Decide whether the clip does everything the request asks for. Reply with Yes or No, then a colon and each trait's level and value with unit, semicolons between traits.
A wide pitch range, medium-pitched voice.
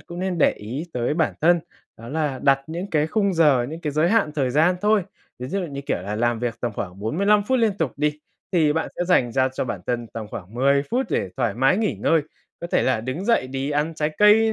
Yes: wide, 5.8 semitones; medium, 150 Hz